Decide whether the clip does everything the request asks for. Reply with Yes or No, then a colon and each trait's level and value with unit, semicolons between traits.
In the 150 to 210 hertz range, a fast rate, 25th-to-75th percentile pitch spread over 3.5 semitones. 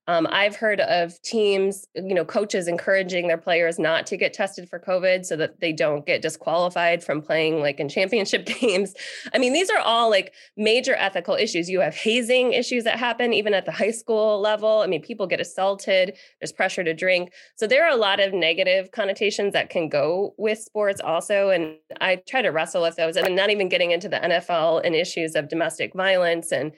Yes: high, 190 Hz; fast, 210 wpm; average, 3.9 semitones